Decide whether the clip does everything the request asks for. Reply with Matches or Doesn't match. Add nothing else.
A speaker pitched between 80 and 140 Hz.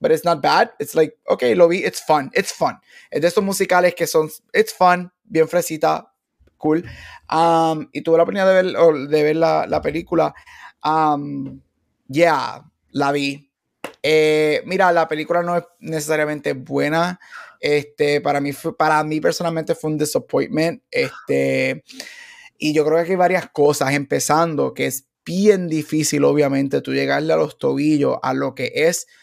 Doesn't match